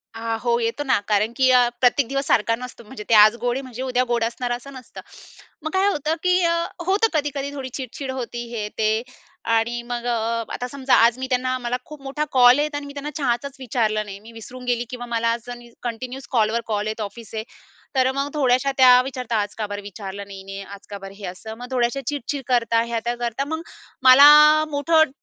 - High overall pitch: Yes, high, 245 Hz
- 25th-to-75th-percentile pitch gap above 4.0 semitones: No, average, 3.2 semitones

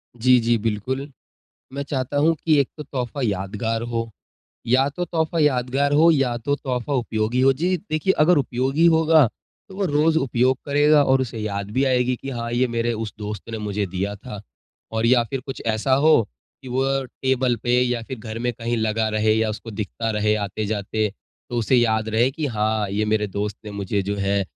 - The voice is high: No, low, 120 Hz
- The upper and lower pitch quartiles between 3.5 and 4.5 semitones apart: Yes, average, 4.0 semitones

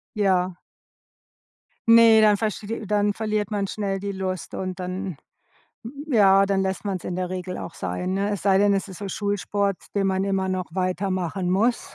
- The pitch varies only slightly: Yes, narrow, 1.7 semitones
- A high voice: Yes, high, 195 Hz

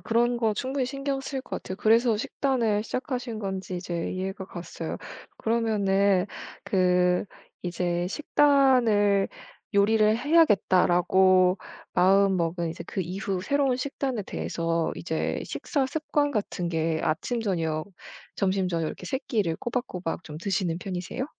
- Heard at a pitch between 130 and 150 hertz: No, high, 195 Hz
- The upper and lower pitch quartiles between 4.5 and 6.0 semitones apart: Yes, average, 5.2 semitones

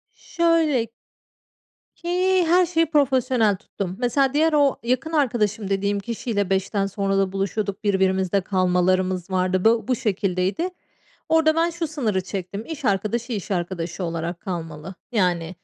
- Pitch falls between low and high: No, high, 205 Hz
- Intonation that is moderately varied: No, wide, 6.6 semitones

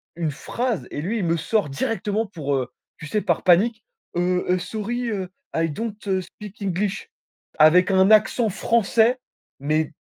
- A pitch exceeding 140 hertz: Yes, high, 190 Hz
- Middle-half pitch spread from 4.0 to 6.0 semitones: Yes, average, 4.6 semitones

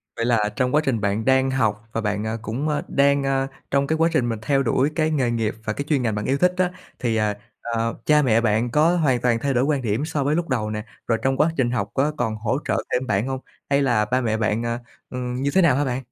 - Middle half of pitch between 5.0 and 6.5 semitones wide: No, average, 3.8 semitones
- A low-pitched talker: Yes, low, 125 Hz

